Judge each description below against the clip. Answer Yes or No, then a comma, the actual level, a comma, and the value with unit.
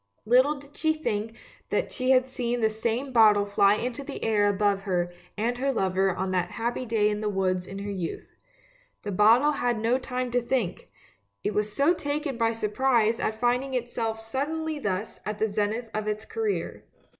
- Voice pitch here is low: No, high, 225 Hz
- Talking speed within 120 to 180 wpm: No, average, 190 wpm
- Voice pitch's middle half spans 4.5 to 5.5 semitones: No, average, 3.7 semitones